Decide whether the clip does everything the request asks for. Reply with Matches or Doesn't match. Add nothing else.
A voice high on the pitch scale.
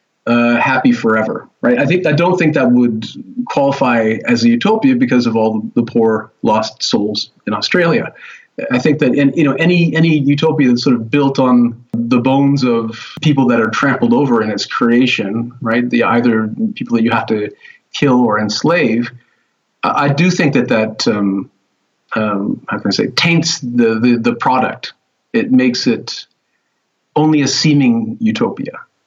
Doesn't match